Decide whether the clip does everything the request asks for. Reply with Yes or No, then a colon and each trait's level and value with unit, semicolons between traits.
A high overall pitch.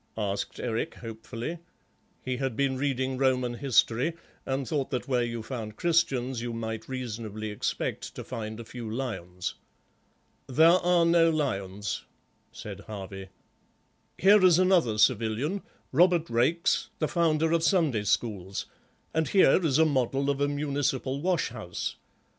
No: low, 130 Hz